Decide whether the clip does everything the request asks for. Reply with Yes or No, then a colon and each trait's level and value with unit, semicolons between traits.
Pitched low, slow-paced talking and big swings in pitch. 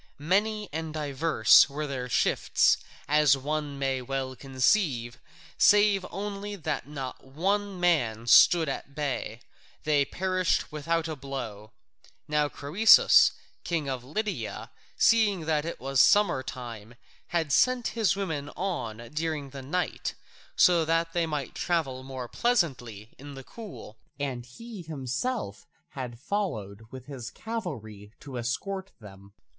No: medium, 145 Hz; slow, 130 wpm; wide, 5.7 semitones